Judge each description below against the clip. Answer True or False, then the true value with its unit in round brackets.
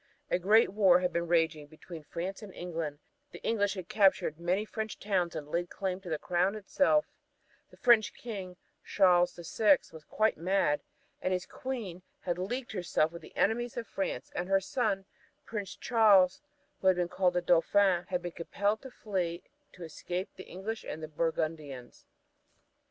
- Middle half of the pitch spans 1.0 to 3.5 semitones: True (3.1 semitones)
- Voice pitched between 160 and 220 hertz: True (185 Hz)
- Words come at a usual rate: True (170 wpm)